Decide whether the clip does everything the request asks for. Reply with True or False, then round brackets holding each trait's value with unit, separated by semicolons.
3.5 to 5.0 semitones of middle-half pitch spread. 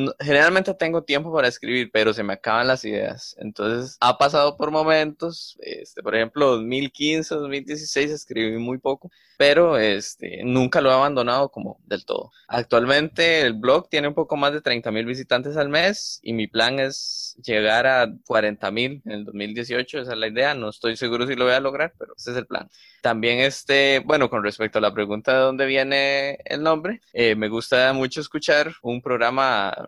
True (4.3 semitones)